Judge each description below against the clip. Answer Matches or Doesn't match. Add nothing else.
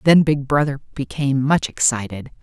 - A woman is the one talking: Matches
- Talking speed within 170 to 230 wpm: Doesn't match